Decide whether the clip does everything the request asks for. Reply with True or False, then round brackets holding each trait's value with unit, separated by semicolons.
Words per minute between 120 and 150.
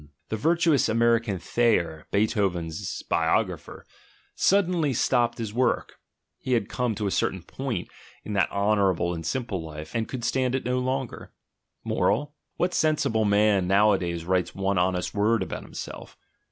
True (145 wpm)